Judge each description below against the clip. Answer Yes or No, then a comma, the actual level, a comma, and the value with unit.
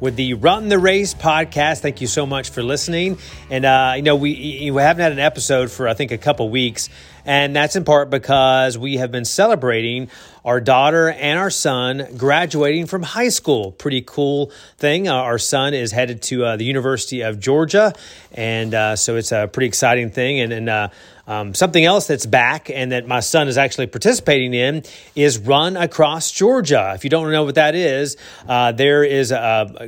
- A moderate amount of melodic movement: Yes, average, 3.6 semitones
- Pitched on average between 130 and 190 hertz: Yes, low, 135 Hz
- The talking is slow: No, average, 200 wpm